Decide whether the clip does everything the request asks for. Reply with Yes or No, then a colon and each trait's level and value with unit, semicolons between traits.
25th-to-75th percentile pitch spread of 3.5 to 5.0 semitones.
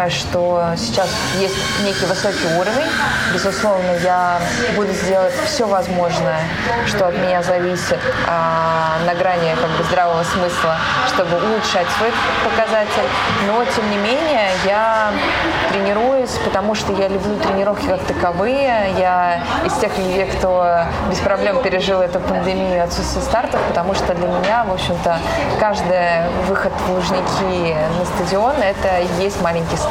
No: narrow, 2.6 semitones